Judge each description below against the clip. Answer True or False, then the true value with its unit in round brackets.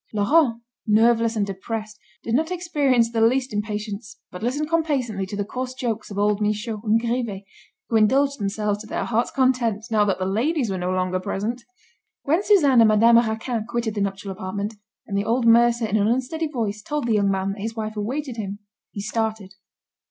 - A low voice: False (225 Hz)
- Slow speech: False (195 wpm)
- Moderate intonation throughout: True (3.2 semitones)